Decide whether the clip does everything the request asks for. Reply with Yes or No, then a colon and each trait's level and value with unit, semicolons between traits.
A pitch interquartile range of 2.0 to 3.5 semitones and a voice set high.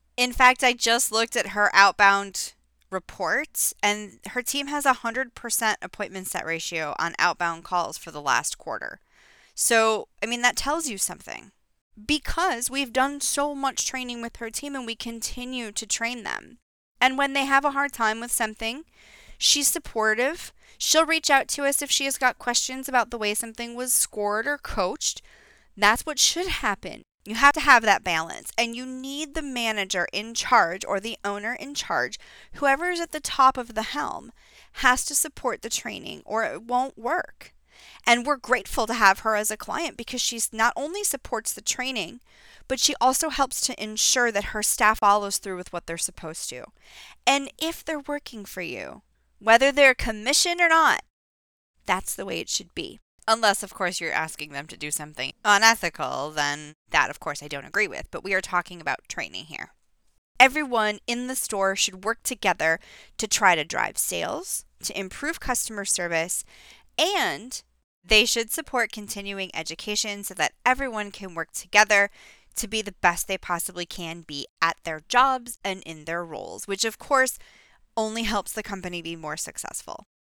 No: average, 5.0 semitones; high, 225 Hz